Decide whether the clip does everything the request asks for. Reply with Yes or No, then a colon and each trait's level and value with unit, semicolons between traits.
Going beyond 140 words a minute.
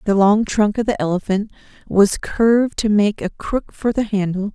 Yes: average, 200 wpm